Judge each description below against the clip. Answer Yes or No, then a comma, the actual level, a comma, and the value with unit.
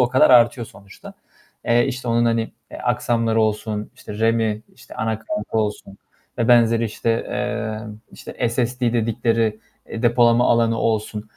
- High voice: No, low, 115 Hz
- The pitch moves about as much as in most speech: No, narrow, 1.4 semitones